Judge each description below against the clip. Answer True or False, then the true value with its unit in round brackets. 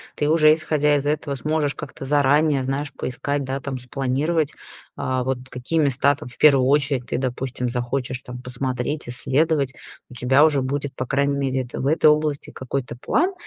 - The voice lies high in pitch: False (140 Hz)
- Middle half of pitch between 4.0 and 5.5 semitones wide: False (2.4 semitones)